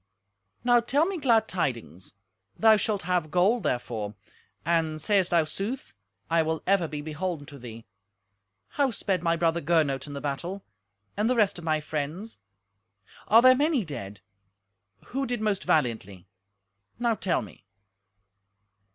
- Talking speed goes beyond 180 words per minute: No, average, 145 wpm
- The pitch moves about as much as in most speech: No, wide, 6.9 semitones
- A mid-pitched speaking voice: Yes, medium, 170 Hz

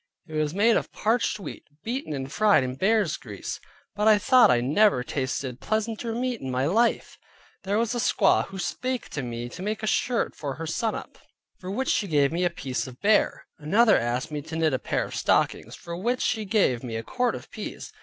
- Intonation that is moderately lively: No, wide, 8.5 semitones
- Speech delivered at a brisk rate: Yes, fast, 215 wpm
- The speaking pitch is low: No, medium, 185 Hz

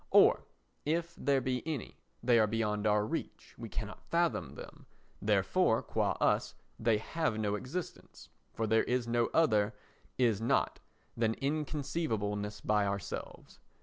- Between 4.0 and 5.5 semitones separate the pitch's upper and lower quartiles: Yes, average, 5.2 semitones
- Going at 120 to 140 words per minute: Yes, slow, 135 wpm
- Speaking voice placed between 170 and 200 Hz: No, low, 115 Hz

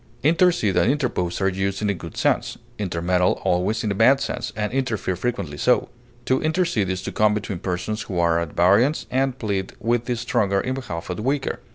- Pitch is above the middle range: No, low, 105 Hz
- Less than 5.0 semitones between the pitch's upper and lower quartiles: No, wide, 5.5 semitones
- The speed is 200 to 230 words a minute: Yes, fast, 205 wpm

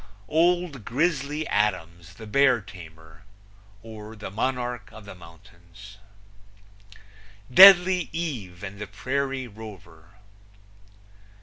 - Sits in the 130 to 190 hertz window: No, low, 110 Hz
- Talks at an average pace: No, slow, 95 wpm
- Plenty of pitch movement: Yes, wide, 6.9 semitones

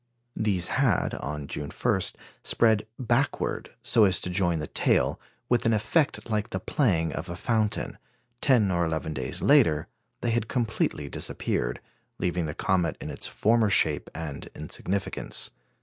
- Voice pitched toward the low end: Yes, very low, 95 Hz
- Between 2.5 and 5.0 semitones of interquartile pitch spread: No, wide, 5.5 semitones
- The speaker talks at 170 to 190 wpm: No, average, 150 wpm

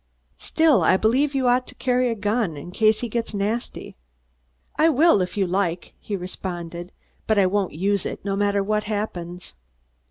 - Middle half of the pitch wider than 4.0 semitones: Yes, average, 4.4 semitones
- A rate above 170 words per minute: Yes, average, 180 wpm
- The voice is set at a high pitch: Yes, high, 205 Hz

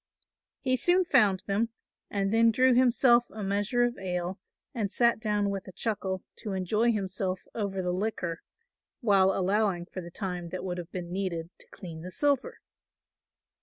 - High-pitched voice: Yes, high, 195 Hz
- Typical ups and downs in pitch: Yes, average, 3.7 semitones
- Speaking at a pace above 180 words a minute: No, average, 165 wpm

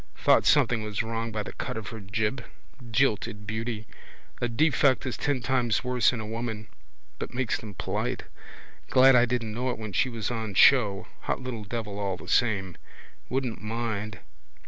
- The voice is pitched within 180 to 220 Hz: No, low, 115 Hz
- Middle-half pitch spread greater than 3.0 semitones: No, narrow, 2.5 semitones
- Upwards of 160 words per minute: Yes, average, 180 wpm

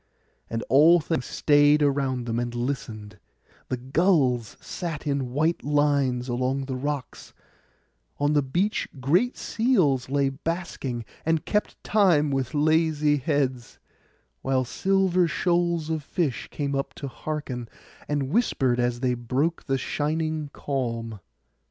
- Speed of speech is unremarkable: No, slow, 125 wpm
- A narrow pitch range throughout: No, average, 3.8 semitones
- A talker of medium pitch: Yes, medium, 145 Hz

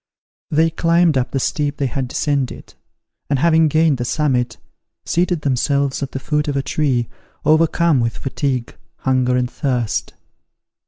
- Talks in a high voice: No, medium, 140 Hz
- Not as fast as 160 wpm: Yes, average, 150 wpm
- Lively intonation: No, average, 3.4 semitones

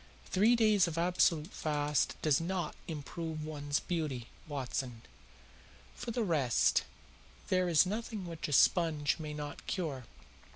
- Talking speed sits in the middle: No, slow, 130 wpm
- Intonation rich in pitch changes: No, average, 3.8 semitones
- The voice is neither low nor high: Yes, medium, 160 Hz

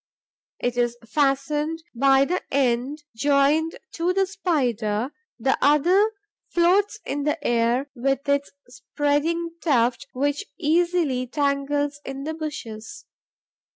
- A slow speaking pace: Yes, slow, 115 wpm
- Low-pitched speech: No, very high, 285 Hz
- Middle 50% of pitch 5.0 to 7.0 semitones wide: No, average, 3.8 semitones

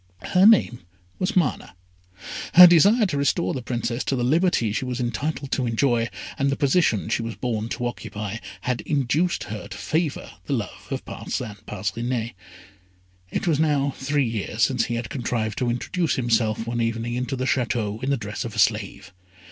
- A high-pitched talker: No, low, 125 Hz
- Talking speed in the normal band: Yes, average, 180 wpm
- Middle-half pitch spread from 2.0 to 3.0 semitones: No, average, 3.8 semitones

